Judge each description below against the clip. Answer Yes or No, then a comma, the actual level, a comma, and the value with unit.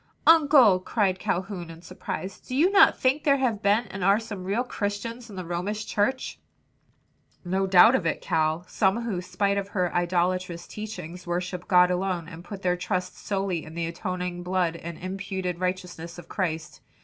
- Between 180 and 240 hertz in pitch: Yes, medium, 185 Hz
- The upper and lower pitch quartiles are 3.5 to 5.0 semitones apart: No, average, 2.7 semitones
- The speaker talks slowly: No, average, 175 wpm